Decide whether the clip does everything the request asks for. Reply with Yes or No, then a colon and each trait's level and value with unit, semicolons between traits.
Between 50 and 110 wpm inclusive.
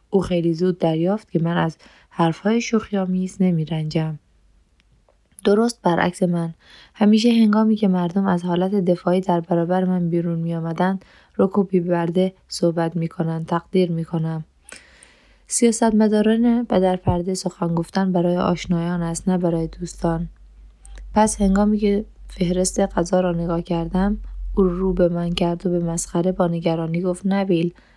No: average, 150 wpm